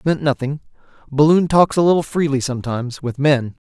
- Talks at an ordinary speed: Yes, average, 180 wpm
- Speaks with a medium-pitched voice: Yes, medium, 145 Hz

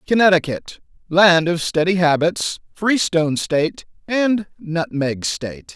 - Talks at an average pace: No, slow, 105 wpm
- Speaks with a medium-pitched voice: Yes, medium, 175 Hz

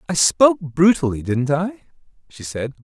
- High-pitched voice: No, medium, 150 Hz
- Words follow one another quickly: No, average, 145 wpm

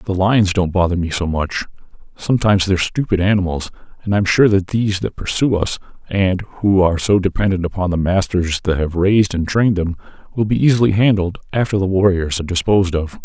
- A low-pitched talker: Yes, very low, 95 Hz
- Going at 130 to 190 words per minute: No, fast, 205 wpm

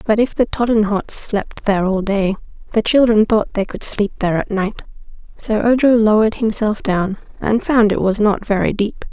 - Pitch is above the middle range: Yes, high, 210 Hz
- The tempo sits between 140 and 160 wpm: No, average, 190 wpm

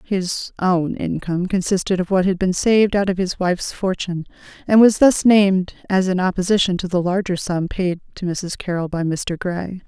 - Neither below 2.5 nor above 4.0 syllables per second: No, 5.2 syllables/s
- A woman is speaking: Yes, female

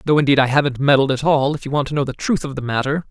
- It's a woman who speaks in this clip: No, male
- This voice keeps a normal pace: No, fast, 330 wpm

